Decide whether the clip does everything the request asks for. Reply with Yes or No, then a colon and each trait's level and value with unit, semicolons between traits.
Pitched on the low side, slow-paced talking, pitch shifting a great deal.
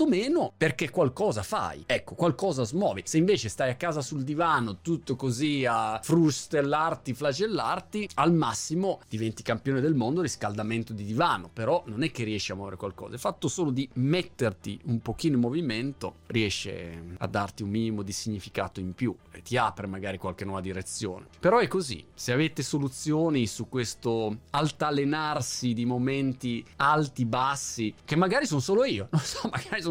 No: low, 125 Hz; average, 165 wpm; wide, 5.9 semitones